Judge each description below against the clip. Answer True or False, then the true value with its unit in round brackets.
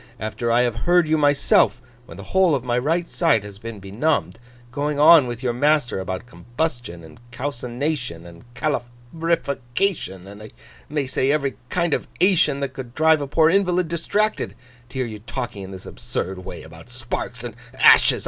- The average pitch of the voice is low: True (125 Hz)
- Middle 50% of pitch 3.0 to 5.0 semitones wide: False (5.6 semitones)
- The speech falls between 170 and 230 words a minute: True (175 wpm)